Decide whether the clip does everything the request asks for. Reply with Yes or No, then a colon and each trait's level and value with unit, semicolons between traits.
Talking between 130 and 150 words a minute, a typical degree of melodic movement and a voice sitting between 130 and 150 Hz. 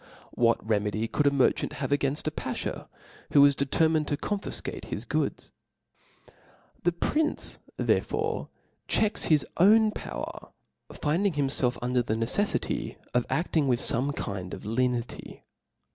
Yes: slow, 135 wpm; average, 4.8 semitones; medium, 140 Hz